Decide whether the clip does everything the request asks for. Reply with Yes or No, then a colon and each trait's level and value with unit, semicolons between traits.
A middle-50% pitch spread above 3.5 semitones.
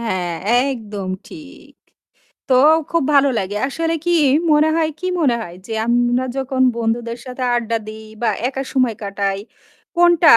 Yes: average, 4.4 semitones